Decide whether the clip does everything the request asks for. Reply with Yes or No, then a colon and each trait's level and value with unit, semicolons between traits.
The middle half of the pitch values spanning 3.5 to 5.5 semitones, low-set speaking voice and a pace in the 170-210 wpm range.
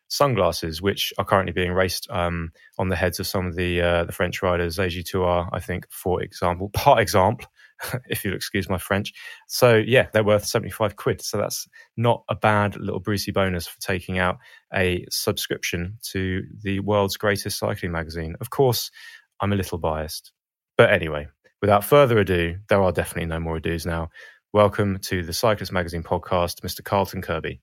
No: average, 2.7 semitones; very low, 95 Hz; average, 180 wpm